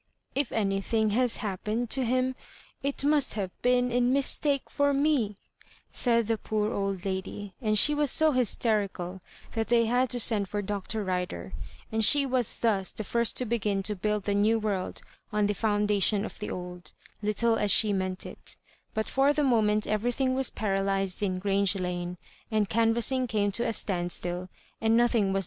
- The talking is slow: No, average, 175 wpm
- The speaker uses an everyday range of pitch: Yes, average, 3.6 semitones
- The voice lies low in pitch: No, high, 215 Hz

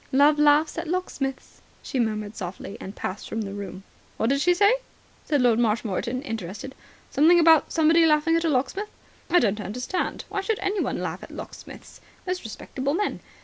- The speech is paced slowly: No, average, 175 wpm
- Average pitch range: No, wide, 7.0 semitones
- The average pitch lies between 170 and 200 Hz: No, very high, 280 Hz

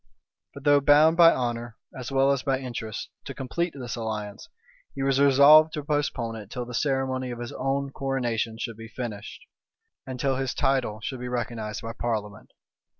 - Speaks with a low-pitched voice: Yes, low, 130 Hz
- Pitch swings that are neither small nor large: Yes, average, 3.1 semitones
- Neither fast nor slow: Yes, average, 180 wpm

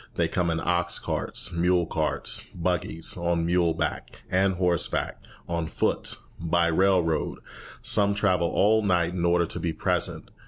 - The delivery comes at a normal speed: Yes, average, 145 wpm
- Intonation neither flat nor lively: No, narrow, 1.5 semitones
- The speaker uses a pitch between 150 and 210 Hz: No, very low, 85 Hz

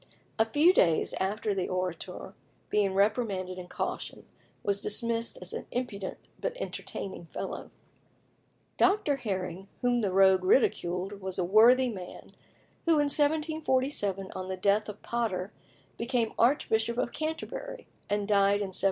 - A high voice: Yes, high, 210 Hz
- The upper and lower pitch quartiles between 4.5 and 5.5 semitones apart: Yes, average, 4.9 semitones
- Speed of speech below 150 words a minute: Yes, average, 140 wpm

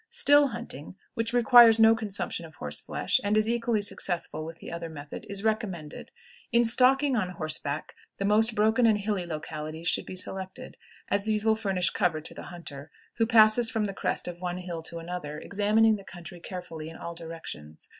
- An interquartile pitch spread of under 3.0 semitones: No, average, 4.9 semitones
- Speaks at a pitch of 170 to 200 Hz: Yes, high, 190 Hz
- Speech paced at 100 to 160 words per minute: No, average, 190 wpm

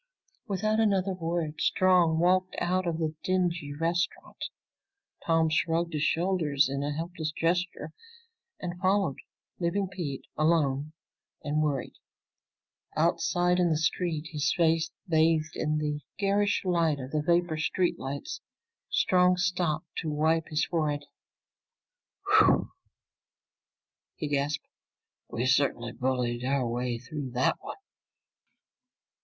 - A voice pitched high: No, medium, 160 Hz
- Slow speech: Yes, slow, 120 wpm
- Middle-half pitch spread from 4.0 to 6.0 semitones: No, average, 3.2 semitones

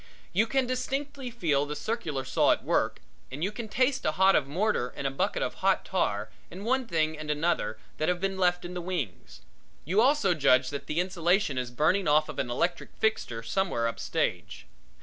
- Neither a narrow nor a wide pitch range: No, wide, 6.6 semitones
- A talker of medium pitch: Yes, medium, 175 Hz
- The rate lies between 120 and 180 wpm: No, fast, 205 wpm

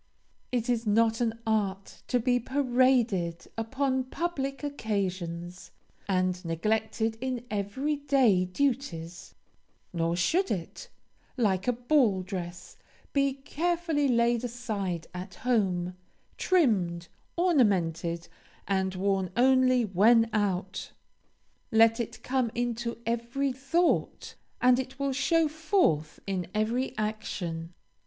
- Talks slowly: Yes, slow, 110 wpm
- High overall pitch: Yes, high, 225 Hz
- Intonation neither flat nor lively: No, wide, 5.8 semitones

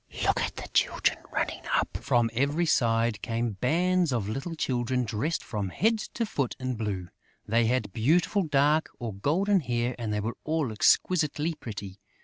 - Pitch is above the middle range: No, low, 125 Hz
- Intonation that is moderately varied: No, wide, 6.0 semitones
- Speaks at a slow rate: No, average, 165 wpm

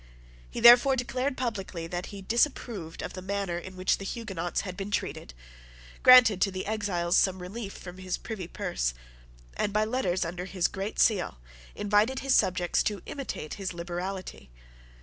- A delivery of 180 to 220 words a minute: No, average, 165 wpm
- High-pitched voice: Yes, high, 195 Hz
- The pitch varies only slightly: No, average, 3.6 semitones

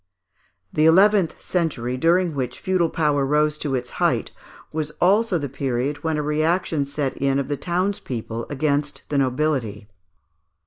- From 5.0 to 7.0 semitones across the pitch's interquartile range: No, average, 3.6 semitones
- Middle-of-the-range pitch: Yes, medium, 150 Hz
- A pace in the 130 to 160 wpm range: Yes, average, 150 wpm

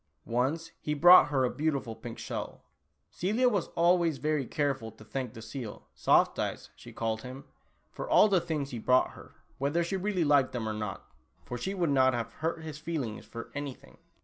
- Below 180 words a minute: No, average, 195 wpm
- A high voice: No, medium, 140 Hz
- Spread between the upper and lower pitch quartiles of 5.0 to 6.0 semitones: Yes, average, 5.3 semitones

